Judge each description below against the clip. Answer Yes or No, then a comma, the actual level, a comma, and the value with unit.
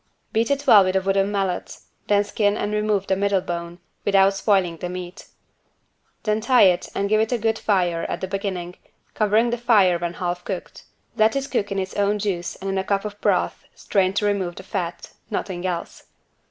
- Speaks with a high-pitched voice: Yes, high, 195 Hz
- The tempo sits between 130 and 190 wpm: No, fast, 205 wpm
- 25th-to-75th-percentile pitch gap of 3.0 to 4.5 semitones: No, narrow, 2.4 semitones